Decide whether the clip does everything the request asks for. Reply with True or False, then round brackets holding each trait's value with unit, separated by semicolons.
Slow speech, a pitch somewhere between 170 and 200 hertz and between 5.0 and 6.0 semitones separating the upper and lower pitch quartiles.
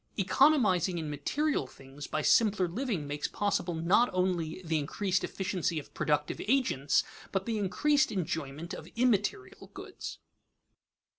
True (130 wpm; 185 Hz; 5.5 semitones)